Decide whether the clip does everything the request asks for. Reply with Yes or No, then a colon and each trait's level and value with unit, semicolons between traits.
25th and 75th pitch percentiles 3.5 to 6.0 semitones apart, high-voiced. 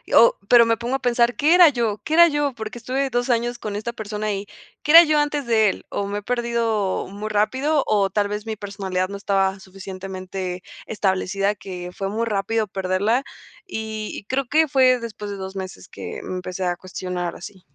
Yes: average, 3.8 semitones; high, 215 Hz